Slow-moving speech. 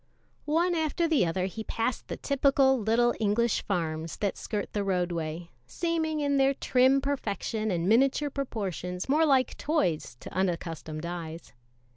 No: average, 145 wpm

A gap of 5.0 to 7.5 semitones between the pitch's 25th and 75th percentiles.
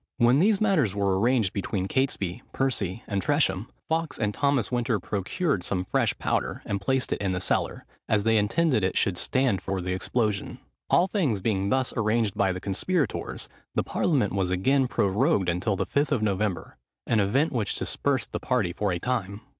Yes: wide, 5.5 semitones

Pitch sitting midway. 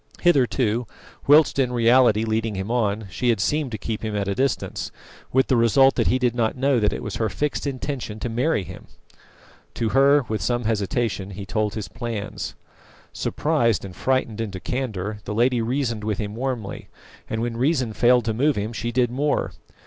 No: low, 115 Hz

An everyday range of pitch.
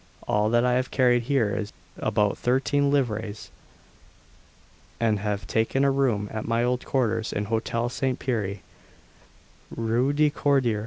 Yes: average, 3.5 semitones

